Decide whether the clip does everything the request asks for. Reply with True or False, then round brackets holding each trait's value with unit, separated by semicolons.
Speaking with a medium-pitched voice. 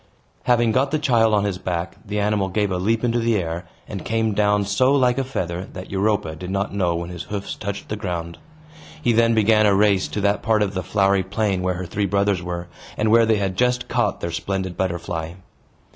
False (100 Hz)